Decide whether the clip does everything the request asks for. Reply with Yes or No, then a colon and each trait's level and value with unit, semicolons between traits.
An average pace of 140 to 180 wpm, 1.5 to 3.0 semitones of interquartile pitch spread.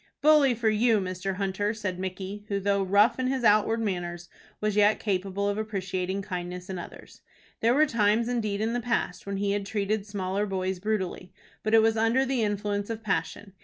No: average, 195 wpm; average, 2.7 semitones